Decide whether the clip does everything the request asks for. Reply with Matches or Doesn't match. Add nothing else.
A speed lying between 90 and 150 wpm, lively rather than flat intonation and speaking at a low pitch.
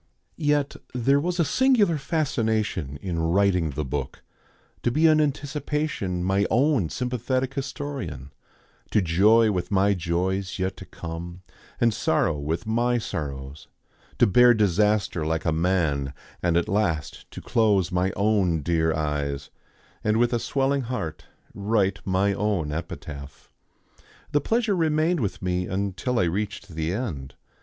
Matches